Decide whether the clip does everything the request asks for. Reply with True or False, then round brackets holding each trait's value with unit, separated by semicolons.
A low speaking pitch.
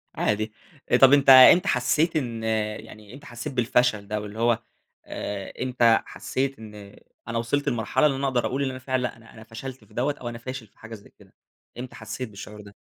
True (120 Hz)